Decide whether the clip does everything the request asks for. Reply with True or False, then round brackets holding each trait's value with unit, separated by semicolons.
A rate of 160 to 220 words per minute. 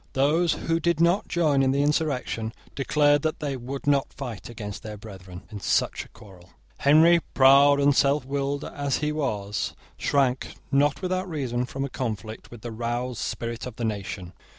True (175 wpm)